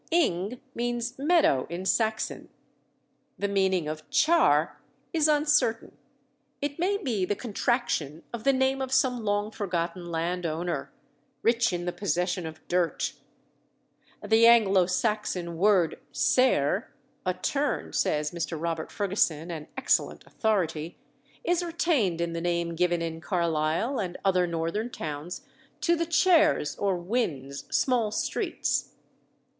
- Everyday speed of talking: No, slow, 130 wpm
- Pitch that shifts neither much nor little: No, wide, 6.3 semitones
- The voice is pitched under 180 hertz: No, high, 190 Hz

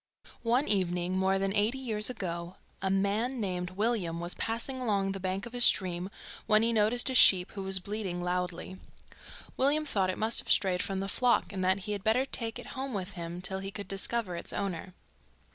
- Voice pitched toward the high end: Yes, high, 195 Hz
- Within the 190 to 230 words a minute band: Yes, fast, 205 wpm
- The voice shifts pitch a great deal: No, average, 3.6 semitones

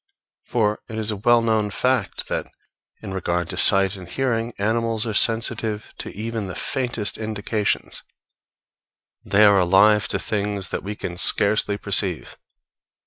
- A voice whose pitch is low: Yes, low, 105 Hz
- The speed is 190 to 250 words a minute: No, average, 145 wpm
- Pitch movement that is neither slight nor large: No, narrow, 2.3 semitones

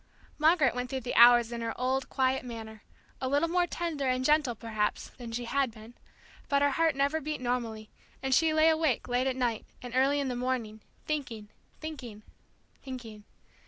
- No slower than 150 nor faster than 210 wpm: Yes, average, 185 wpm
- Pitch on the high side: Yes, very high, 255 Hz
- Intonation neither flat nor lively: Yes, average, 3.5 semitones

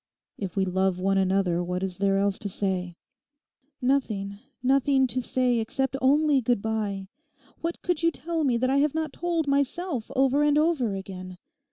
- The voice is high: Yes, high, 245 Hz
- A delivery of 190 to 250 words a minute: No, average, 175 wpm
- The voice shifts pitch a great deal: Yes, wide, 6.4 semitones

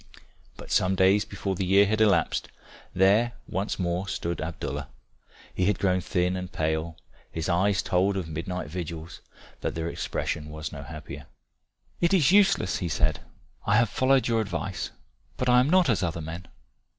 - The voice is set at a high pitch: No, very low, 95 Hz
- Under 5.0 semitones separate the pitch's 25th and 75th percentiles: Yes, average, 3.7 semitones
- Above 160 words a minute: Yes, average, 170 wpm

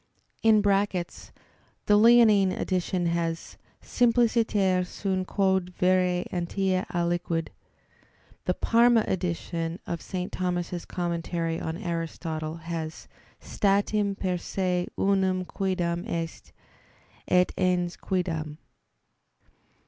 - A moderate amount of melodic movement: No, narrow, 2.3 semitones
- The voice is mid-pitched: Yes, medium, 180 Hz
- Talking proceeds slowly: Yes, slow, 90 wpm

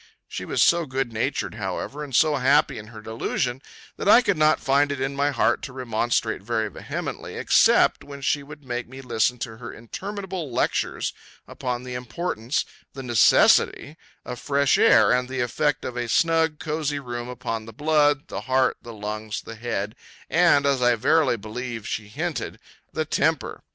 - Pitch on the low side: Yes, low, 130 Hz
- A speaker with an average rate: Yes, average, 175 wpm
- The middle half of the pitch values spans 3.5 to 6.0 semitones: Yes, average, 3.8 semitones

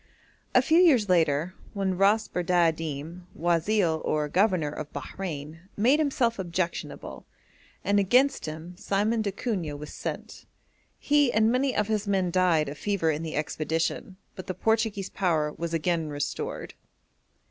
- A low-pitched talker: No, medium, 180 Hz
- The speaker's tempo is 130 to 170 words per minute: Yes, average, 140 wpm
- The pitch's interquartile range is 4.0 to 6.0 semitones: Yes, average, 4.8 semitones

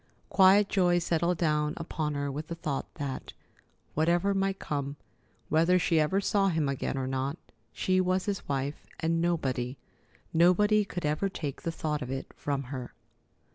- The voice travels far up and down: No, average, 4.3 semitones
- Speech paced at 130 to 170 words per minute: Yes, average, 165 wpm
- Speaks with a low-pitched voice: No, medium, 160 Hz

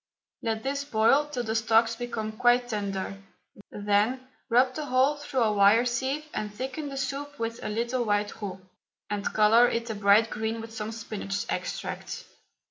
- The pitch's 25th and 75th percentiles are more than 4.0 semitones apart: No, average, 3.2 semitones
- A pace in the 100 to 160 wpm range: No, average, 170 wpm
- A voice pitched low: No, high, 230 Hz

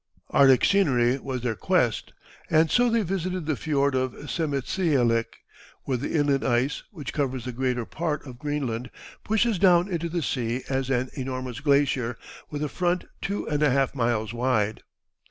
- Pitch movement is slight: No, average, 4.2 semitones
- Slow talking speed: No, average, 165 wpm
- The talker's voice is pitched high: No, medium, 140 Hz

